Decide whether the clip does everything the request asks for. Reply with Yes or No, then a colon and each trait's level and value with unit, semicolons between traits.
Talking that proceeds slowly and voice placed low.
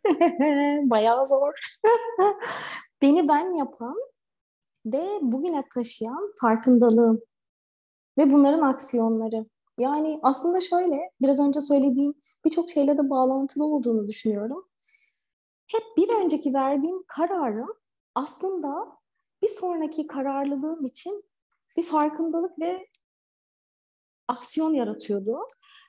No: slow, 90 wpm; very high, 290 Hz